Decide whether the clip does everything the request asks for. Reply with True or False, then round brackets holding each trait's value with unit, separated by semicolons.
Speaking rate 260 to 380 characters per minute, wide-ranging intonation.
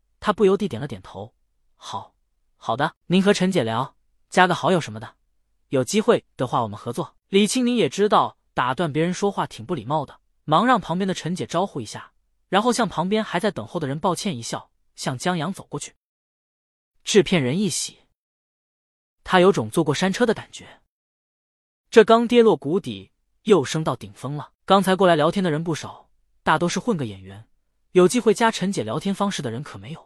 True (280 characters per minute; 6.6 semitones)